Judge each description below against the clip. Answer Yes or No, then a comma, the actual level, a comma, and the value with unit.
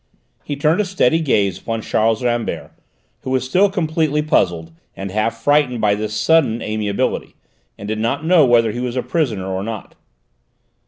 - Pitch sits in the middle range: No, low, 120 Hz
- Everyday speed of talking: Yes, average, 170 wpm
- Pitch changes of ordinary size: No, wide, 5.9 semitones